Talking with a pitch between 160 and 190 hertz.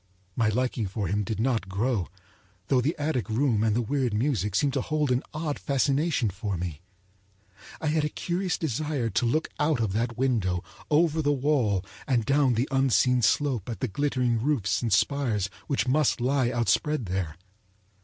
No: low, 125 Hz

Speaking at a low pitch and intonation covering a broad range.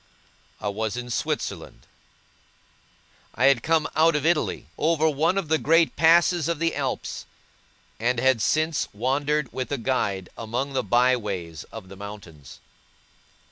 Yes: low, 130 Hz; wide, 6.0 semitones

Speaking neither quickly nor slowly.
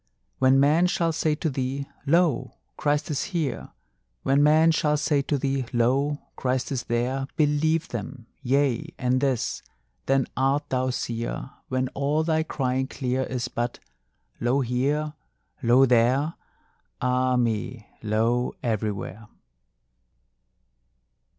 No: slow, 125 wpm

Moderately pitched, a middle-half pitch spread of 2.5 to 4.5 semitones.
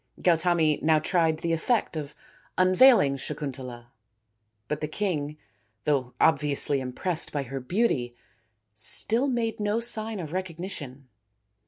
No: medium, 155 Hz; average, 5.1 semitones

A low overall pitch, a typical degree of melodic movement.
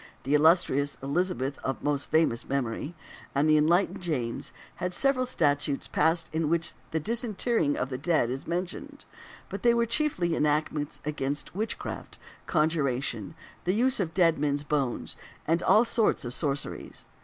No: medium, 155 Hz; average, 4.2 semitones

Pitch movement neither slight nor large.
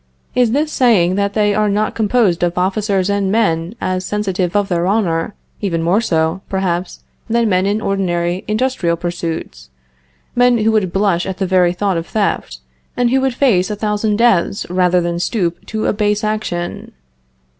Yes: average, 3.5 semitones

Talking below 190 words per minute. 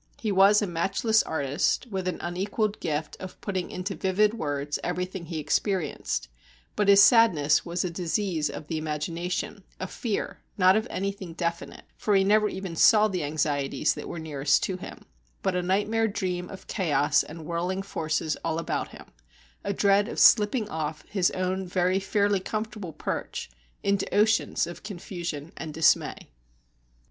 Yes: average, 160 wpm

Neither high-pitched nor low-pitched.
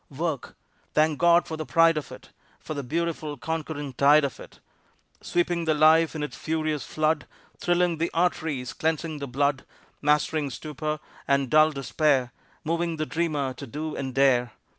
Yes: medium, 155 Hz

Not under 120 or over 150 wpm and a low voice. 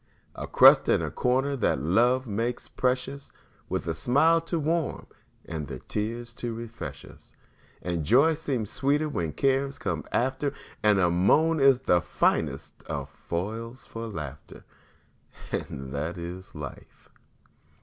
Yes: average, 140 wpm; low, 115 Hz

